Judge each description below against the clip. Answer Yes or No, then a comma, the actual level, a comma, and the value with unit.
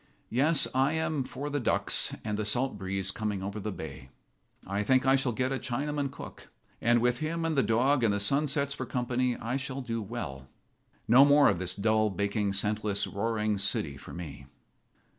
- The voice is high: No, low, 115 Hz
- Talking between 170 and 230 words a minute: Yes, average, 190 wpm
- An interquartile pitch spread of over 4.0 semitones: Yes, average, 5.0 semitones